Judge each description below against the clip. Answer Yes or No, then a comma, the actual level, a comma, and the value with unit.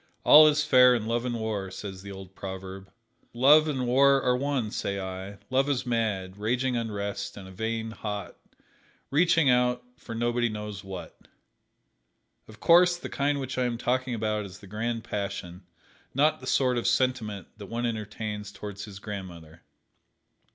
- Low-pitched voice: Yes, low, 115 Hz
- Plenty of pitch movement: No, average, 4.1 semitones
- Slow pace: No, average, 165 wpm